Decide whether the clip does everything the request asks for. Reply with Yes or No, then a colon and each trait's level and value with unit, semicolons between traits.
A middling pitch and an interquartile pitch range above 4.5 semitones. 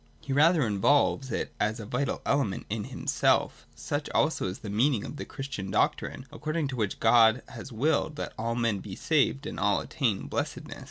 No: low, 120 Hz; average, 5.2 semitones